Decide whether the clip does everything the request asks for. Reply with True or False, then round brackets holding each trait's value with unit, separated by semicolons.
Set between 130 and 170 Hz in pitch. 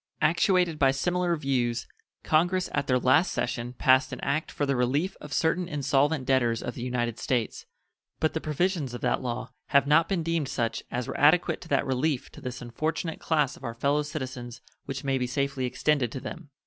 True (140 Hz)